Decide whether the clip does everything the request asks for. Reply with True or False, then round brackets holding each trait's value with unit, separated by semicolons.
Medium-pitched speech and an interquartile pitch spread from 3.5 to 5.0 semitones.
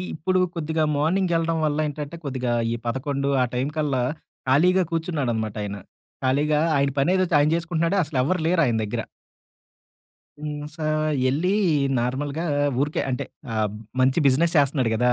True (145 Hz; 4.1 semitones)